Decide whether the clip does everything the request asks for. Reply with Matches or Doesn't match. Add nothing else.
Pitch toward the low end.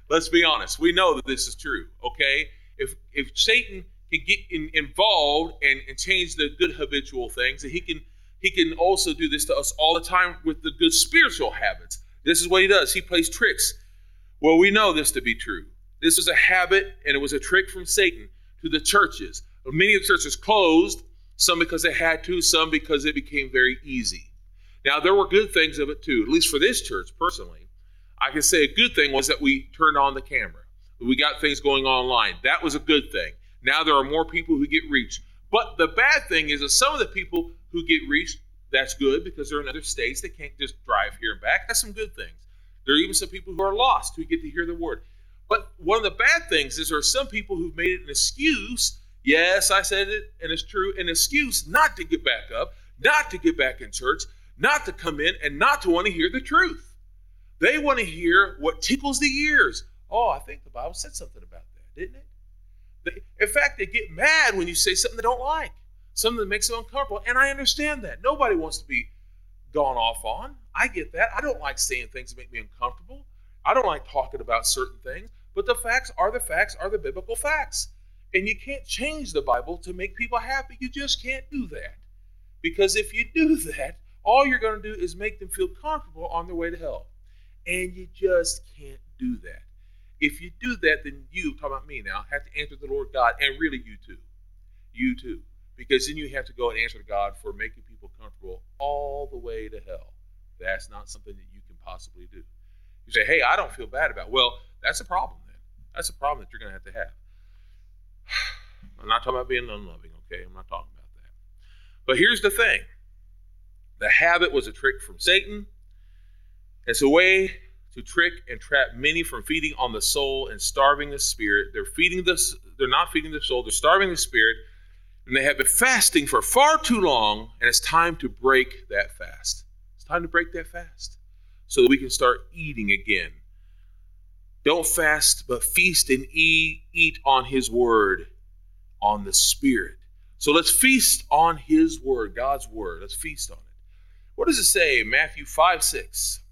Doesn't match